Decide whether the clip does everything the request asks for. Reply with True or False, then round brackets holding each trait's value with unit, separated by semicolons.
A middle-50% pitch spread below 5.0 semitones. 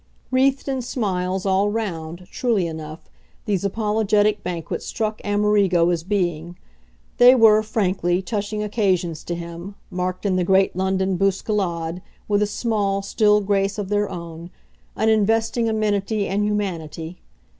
True (2.9 semitones)